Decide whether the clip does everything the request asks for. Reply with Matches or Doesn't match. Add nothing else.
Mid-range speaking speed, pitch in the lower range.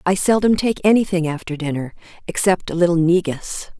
Doesn't match